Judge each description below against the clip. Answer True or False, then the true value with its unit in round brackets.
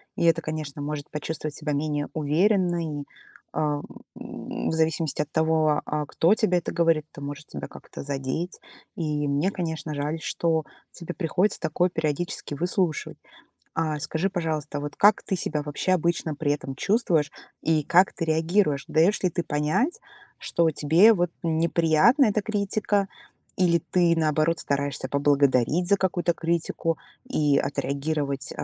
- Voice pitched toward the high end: False (160 Hz)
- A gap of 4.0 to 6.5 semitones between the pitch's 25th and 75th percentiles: False (2.9 semitones)